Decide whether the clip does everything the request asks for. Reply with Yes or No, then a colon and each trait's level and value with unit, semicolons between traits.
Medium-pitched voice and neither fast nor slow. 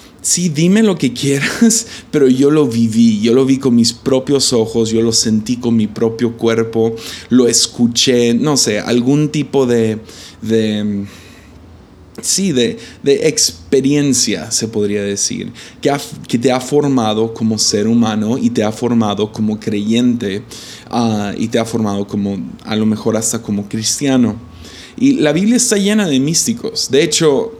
No: low, 115 Hz; average, 160 wpm